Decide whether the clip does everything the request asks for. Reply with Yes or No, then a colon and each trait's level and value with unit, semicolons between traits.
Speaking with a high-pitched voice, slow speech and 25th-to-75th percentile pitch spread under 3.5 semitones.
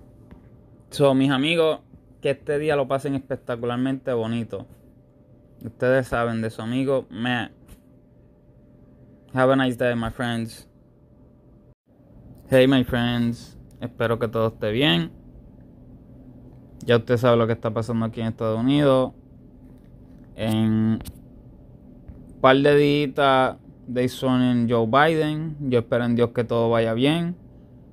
No: low, 125 Hz; slow, 125 wpm; narrow, 2.5 semitones